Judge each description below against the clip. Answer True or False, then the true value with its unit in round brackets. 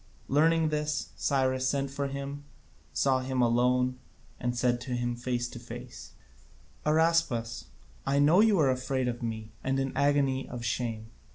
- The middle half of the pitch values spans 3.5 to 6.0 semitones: False (2.7 semitones)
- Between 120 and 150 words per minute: False (165 wpm)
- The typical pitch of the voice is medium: False (130 Hz)